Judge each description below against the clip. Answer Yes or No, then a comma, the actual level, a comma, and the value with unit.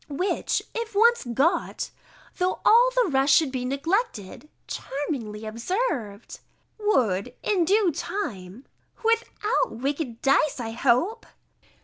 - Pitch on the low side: No, very high, 290 Hz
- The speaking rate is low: Yes, slow, 115 wpm